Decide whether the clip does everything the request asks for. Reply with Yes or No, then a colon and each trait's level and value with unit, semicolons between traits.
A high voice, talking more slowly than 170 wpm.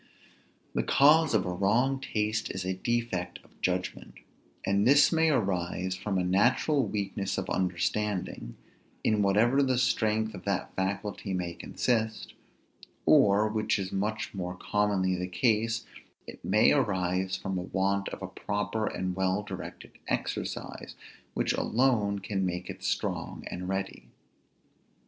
No: low, 100 Hz; average, 140 wpm